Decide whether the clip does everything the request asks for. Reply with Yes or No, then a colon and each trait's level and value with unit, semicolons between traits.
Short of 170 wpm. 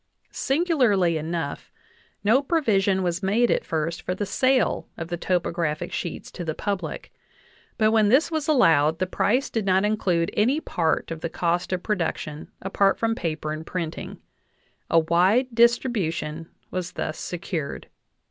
Yes: average, 150 wpm